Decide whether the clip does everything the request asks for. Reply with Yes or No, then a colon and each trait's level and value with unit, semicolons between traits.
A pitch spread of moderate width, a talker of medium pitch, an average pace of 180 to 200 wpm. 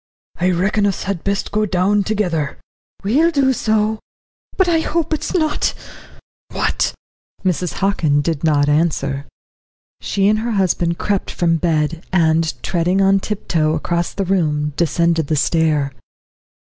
No: average, 4.4 semitones; medium, 180 Hz; average, 145 wpm